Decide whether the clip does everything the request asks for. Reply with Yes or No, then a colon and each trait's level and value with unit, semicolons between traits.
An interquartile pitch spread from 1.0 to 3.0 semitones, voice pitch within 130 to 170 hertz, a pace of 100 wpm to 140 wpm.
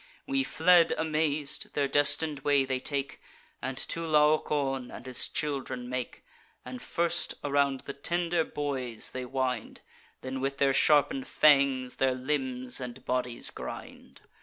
Yes: average, 2.7 semitones; medium, 140 Hz; slow, 135 wpm